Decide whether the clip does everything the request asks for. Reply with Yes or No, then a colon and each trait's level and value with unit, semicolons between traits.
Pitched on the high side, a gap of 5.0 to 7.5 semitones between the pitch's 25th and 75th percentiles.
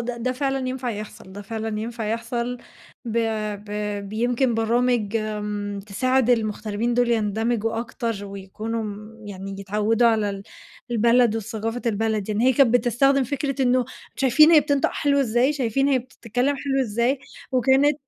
No: high, 235 Hz; average, 3.0 semitones